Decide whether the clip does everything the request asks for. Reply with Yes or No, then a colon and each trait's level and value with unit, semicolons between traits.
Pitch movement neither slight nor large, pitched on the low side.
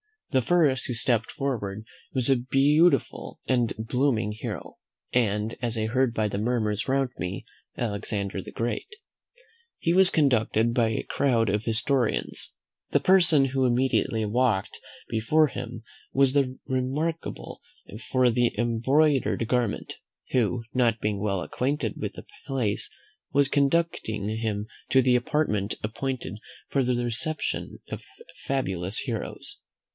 Yes: average, 3.7 semitones; low, 120 Hz